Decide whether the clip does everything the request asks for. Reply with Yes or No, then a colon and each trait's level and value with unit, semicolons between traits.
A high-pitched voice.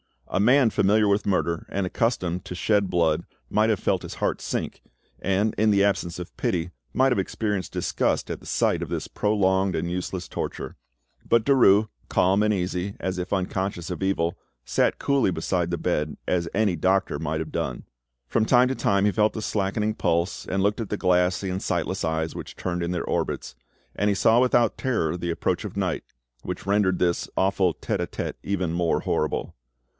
No: very low, 95 Hz